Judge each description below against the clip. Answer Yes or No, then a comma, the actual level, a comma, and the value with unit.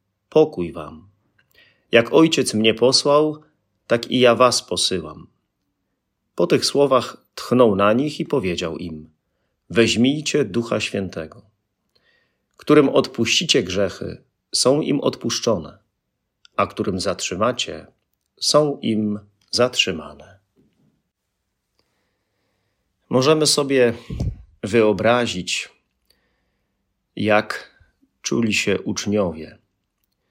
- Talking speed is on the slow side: Yes, slow, 85 wpm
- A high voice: No, low, 105 Hz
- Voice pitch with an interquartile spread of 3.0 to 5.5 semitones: Yes, average, 4.7 semitones